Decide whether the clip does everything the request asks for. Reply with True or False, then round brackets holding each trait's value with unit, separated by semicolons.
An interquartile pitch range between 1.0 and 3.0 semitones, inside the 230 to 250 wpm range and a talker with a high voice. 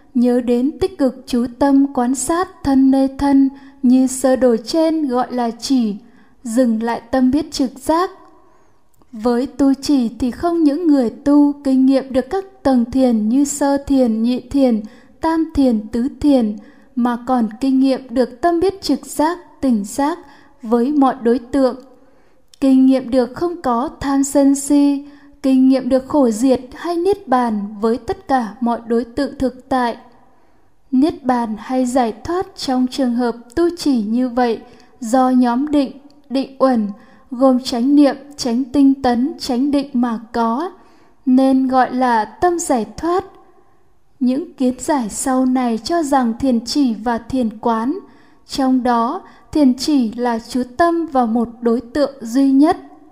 False (2.7 semitones; 165 wpm; 265 Hz)